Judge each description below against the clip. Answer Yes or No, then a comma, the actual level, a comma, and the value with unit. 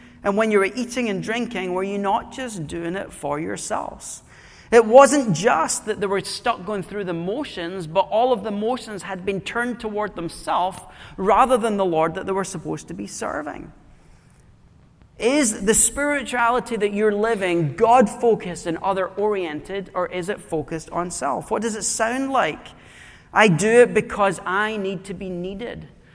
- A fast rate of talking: No, average, 180 wpm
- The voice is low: No, high, 205 Hz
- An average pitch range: Yes, average, 3.8 semitones